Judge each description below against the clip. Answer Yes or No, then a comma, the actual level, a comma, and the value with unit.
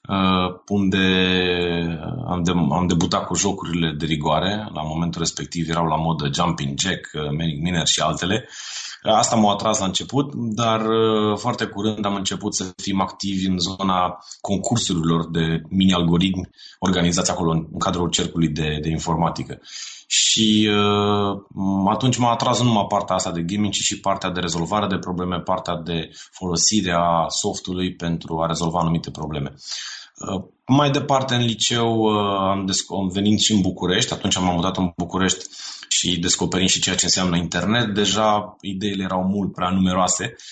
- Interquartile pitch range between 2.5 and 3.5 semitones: Yes, average, 3.2 semitones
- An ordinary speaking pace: Yes, average, 155 wpm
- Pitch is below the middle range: Yes, very low, 95 Hz